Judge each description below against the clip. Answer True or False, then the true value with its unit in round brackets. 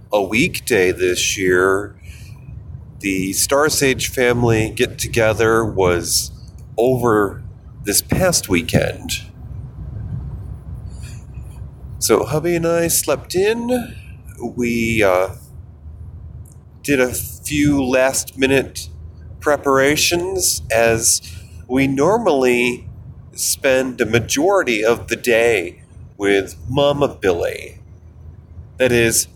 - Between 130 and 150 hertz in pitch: False (115 Hz)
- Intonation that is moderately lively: False (5.7 semitones)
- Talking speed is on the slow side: True (85 wpm)